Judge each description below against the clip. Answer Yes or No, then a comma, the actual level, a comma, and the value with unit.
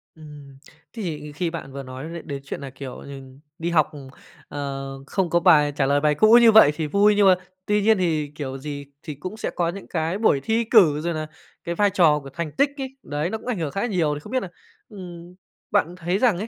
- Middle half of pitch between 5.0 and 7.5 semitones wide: Yes, average, 5.3 semitones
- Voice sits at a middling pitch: Yes, medium, 165 Hz